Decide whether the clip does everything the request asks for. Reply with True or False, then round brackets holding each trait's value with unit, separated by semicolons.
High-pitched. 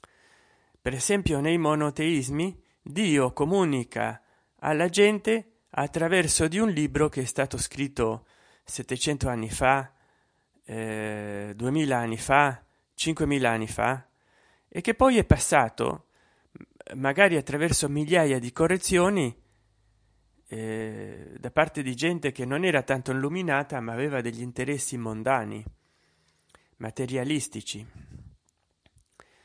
False (135 Hz)